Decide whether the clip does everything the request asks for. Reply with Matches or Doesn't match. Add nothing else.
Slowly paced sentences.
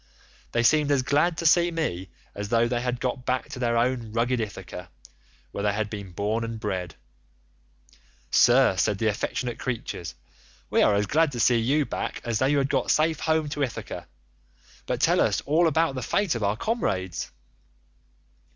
Doesn't match